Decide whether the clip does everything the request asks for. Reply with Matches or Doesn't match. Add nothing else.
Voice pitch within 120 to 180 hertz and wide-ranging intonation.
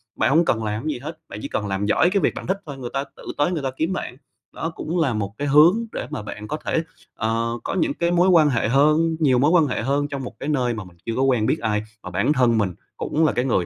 Matches